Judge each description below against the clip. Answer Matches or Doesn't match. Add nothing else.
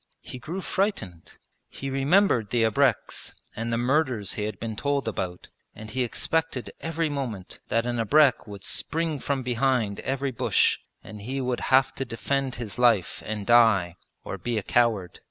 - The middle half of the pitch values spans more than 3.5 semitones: Matches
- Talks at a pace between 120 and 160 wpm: Doesn't match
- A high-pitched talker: Doesn't match